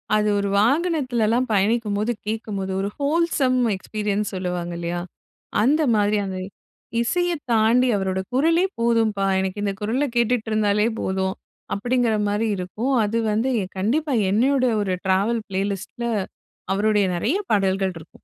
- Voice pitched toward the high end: Yes, high, 215 Hz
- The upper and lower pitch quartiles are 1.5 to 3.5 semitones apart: No, average, 4.1 semitones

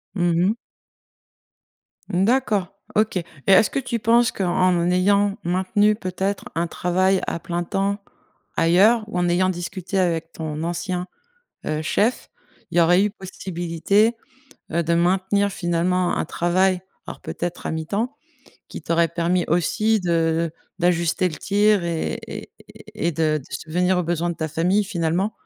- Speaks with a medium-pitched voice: Yes, medium, 180 Hz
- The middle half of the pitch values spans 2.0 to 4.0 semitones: Yes, average, 2.8 semitones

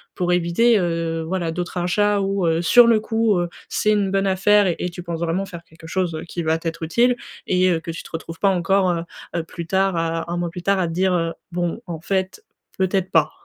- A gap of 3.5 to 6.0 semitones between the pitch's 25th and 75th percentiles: No, average, 2.7 semitones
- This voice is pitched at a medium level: Yes, medium, 180 Hz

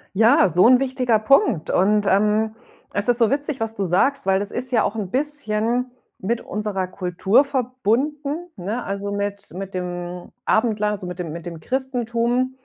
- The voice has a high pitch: Yes, high, 215 Hz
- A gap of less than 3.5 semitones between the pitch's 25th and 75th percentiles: No, average, 4.5 semitones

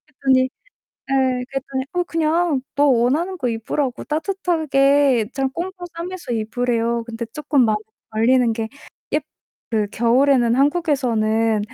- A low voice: No, very high, 260 Hz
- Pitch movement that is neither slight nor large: Yes, average, 4.5 semitones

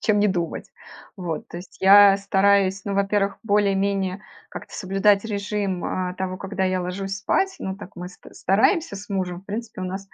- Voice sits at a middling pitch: No, high, 195 Hz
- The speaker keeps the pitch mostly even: Yes, narrow, 1.4 semitones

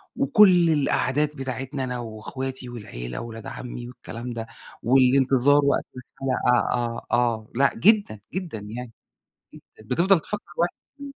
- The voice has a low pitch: Yes, low, 130 Hz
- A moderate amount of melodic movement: Yes, average, 3.8 semitones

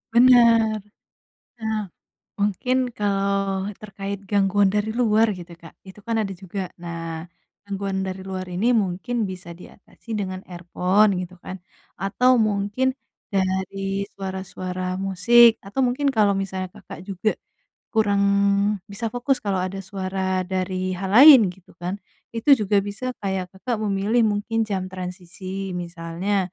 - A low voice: No, high, 195 Hz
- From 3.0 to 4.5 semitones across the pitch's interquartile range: No, narrow, 2.5 semitones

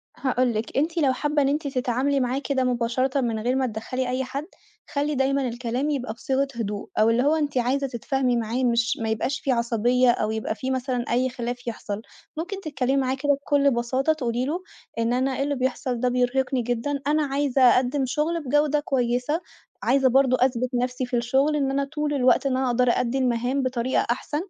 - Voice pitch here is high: Yes, very high, 260 Hz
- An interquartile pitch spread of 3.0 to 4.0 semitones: No, narrow, 2.4 semitones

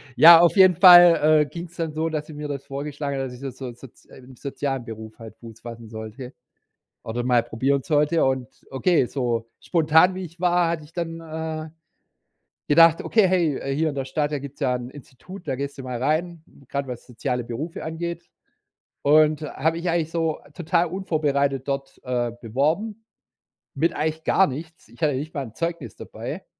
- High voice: No, medium, 150 Hz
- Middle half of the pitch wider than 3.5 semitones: Yes, average, 4.1 semitones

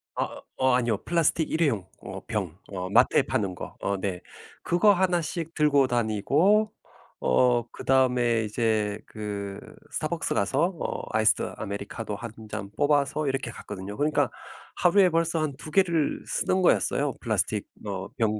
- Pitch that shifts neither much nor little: No, wide, 7.0 semitones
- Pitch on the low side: Yes, low, 120 Hz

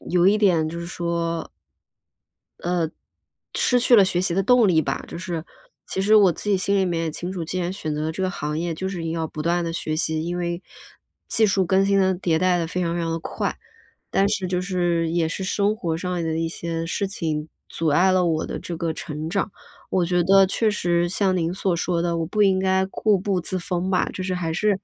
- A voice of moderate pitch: Yes, medium, 175 Hz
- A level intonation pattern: Yes, narrow, 2.3 semitones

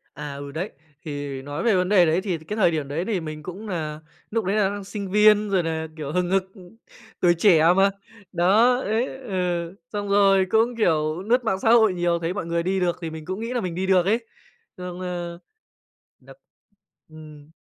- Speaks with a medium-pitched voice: Yes, medium, 180 Hz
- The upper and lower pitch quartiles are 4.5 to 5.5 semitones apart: No, average, 4.1 semitones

